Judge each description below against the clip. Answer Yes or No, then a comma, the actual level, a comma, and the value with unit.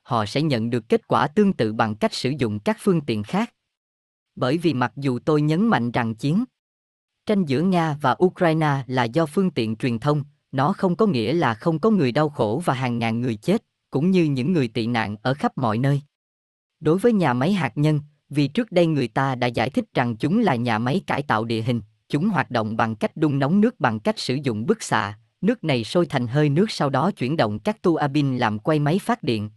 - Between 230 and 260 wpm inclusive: Yes, average, 235 wpm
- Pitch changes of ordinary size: No, wide, 6.4 semitones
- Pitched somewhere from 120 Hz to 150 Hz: Yes, medium, 140 Hz